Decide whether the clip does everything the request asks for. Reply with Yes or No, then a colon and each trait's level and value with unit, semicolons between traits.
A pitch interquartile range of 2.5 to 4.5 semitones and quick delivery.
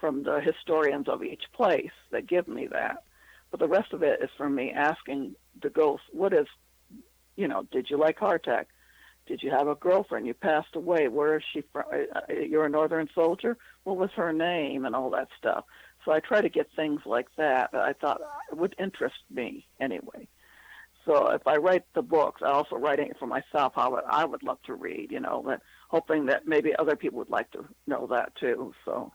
Yes: average, 3.7 semitones; fast, 210 wpm